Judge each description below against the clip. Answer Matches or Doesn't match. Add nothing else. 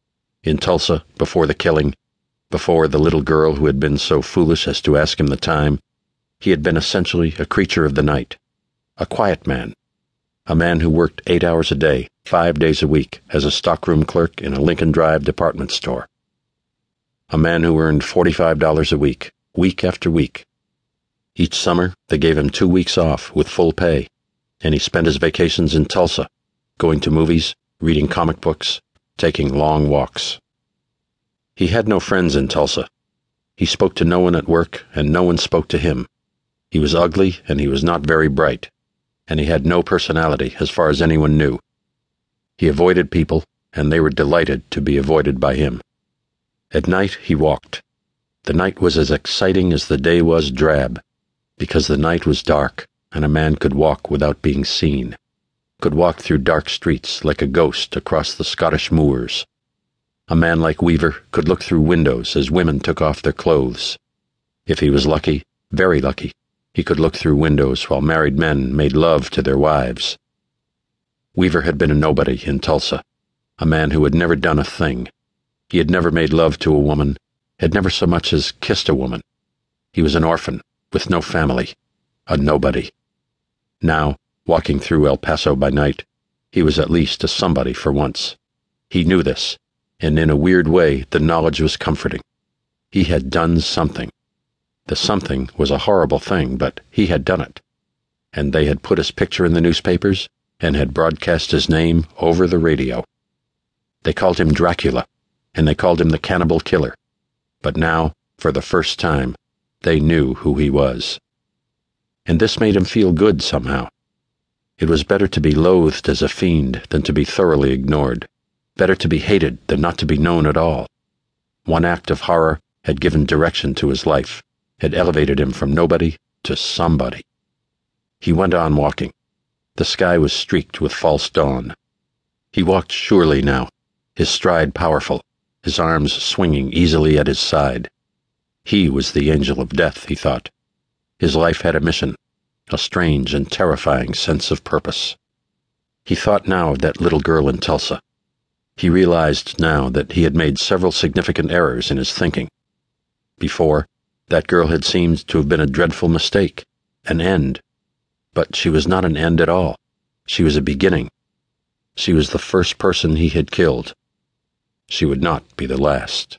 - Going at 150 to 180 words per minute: Matches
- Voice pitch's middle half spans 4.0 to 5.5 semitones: Doesn't match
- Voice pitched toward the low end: Matches